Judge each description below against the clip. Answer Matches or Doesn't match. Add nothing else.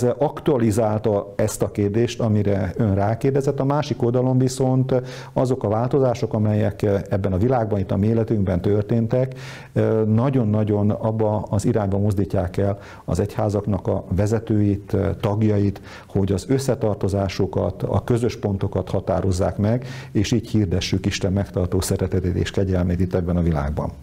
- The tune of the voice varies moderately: Matches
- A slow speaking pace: Doesn't match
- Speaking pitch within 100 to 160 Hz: Matches